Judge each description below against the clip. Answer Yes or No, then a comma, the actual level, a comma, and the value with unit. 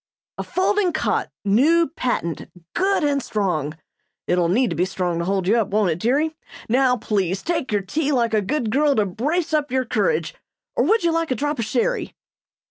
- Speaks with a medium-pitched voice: No, very high, 250 Hz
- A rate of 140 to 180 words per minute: No, average, 200 wpm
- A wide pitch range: Yes, wide, 8.0 semitones